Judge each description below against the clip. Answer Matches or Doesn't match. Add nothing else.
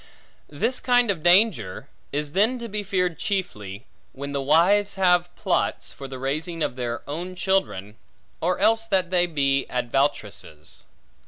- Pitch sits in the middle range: Matches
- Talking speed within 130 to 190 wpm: Matches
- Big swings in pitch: Matches